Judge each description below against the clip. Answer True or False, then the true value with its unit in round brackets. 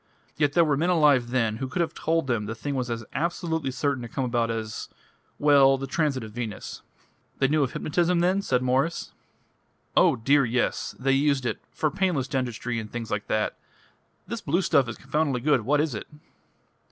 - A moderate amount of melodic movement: True (4.3 semitones)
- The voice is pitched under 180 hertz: True (135 Hz)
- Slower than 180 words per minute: False (190 wpm)